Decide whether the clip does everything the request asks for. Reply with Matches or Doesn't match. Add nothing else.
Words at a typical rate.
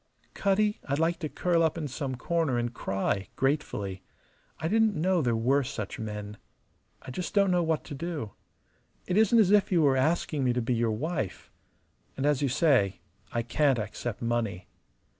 Matches